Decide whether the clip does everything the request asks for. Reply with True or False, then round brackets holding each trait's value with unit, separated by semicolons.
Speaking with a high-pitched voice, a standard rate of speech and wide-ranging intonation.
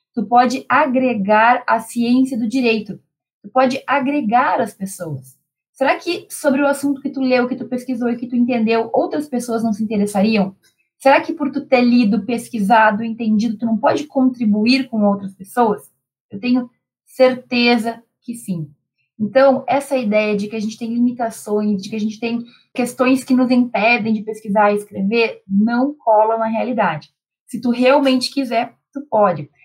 False (235 Hz; 170 wpm; 3.2 semitones)